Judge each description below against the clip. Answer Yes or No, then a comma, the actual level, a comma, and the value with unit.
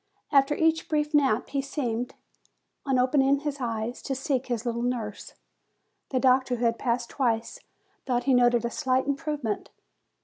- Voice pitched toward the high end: Yes, very high, 255 Hz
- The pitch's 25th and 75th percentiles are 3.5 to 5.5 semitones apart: No, narrow, 2.6 semitones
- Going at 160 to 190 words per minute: Yes, average, 170 wpm